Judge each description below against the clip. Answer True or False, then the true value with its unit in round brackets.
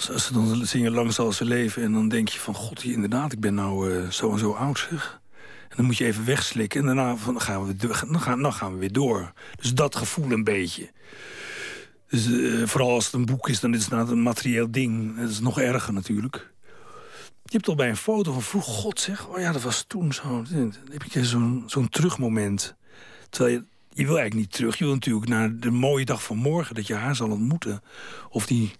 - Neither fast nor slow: False (235 wpm)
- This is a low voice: True (120 Hz)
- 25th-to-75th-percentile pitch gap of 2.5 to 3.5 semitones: False (4.0 semitones)